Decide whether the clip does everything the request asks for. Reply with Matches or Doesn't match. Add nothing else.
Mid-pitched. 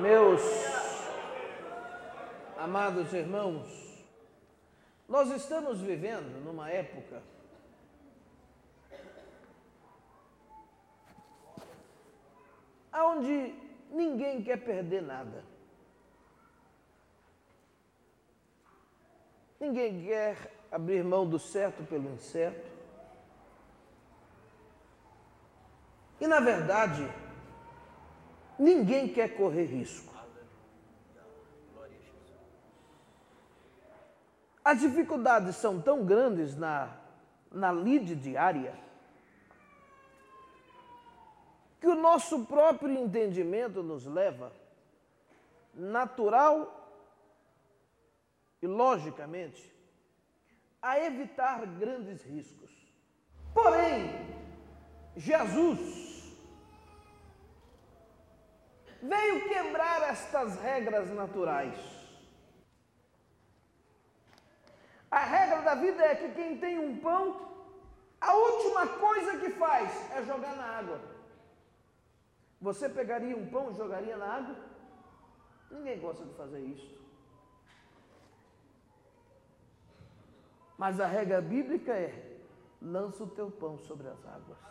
Doesn't match